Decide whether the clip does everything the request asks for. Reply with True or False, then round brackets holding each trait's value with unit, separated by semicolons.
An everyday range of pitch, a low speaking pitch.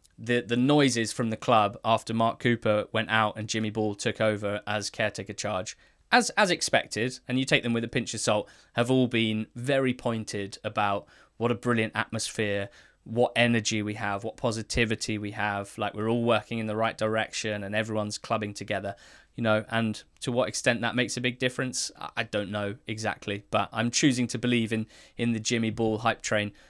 False (2.2 semitones; 110 Hz)